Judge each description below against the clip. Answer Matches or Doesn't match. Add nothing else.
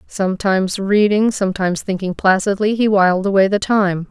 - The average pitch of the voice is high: Matches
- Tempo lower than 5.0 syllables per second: Doesn't match